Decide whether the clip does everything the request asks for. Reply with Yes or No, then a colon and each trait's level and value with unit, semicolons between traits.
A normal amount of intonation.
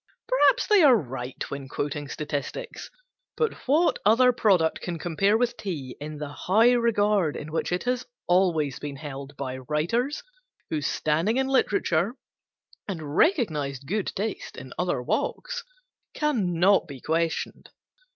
No: wide, 8.0 semitones